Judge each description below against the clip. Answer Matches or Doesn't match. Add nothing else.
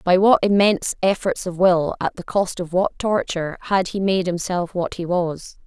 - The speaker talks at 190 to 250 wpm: Matches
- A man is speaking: Doesn't match